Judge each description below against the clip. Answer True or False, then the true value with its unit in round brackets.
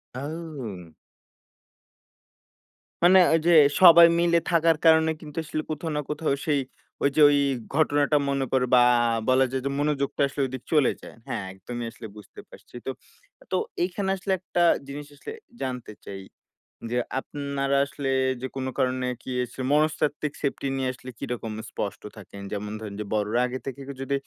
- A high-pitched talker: False (140 Hz)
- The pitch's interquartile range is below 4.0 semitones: True (3.5 semitones)